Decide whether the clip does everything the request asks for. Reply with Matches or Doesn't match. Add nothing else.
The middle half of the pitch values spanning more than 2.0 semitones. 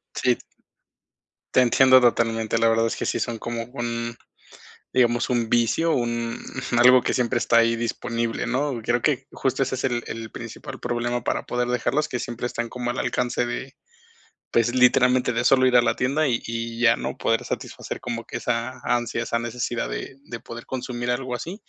Doesn't match